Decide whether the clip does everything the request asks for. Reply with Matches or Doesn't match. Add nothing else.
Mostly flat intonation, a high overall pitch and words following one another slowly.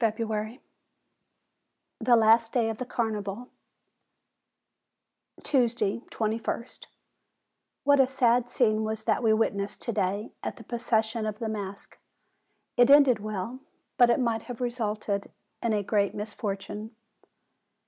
Matches